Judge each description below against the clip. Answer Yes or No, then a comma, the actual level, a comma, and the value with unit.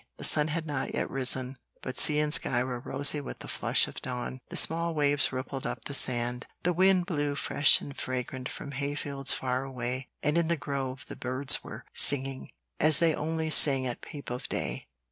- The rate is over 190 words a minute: Yes, average, 200 wpm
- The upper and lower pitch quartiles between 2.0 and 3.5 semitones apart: Yes, average, 2.7 semitones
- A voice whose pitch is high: No, medium, 140 Hz